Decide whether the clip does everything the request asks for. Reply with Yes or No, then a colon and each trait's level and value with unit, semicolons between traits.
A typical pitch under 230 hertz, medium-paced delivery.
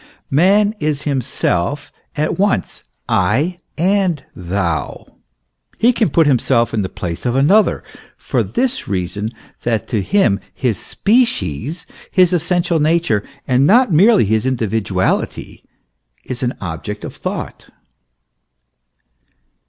No: medium, 140 Hz; slow, 115 wpm